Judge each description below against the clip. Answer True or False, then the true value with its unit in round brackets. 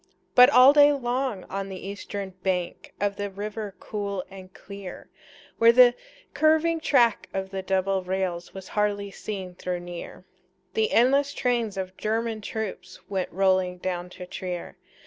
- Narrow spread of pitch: False (3.9 semitones)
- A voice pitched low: False (200 Hz)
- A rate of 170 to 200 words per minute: False (150 wpm)